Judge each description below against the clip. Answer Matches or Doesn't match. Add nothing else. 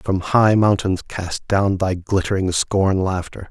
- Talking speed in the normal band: Matches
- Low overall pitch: Matches